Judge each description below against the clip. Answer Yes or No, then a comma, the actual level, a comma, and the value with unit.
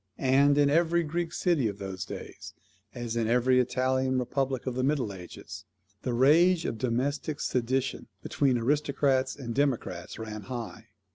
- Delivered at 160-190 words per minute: No, average, 150 wpm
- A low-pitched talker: Yes, low, 130 Hz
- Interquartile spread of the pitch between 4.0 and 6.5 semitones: No, average, 3.3 semitones